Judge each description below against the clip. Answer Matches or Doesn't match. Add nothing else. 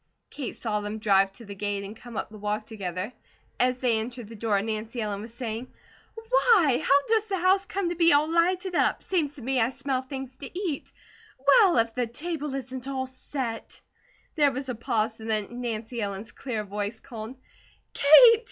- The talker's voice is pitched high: Matches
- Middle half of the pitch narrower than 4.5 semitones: Doesn't match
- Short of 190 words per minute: Doesn't match